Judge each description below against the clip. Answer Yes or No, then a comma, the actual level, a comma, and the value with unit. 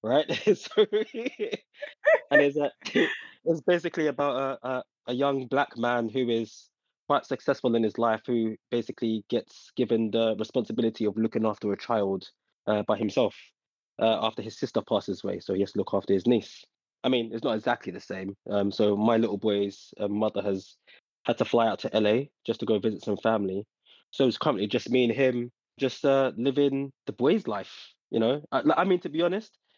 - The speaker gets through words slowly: No, average, 195 wpm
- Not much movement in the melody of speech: No, average, 4.5 semitones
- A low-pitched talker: Yes, low, 120 Hz